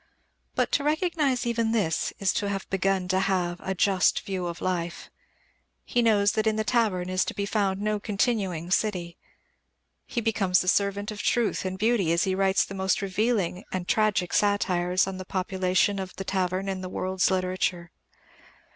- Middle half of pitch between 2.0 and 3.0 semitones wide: Yes, narrow, 2.4 semitones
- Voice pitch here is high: Yes, high, 195 Hz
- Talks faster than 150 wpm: Yes, average, 180 wpm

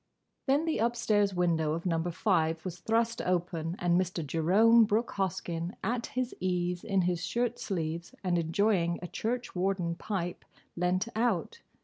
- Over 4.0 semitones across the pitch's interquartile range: Yes, average, 4.5 semitones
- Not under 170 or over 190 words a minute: No, average, 150 wpm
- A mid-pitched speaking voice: Yes, medium, 180 Hz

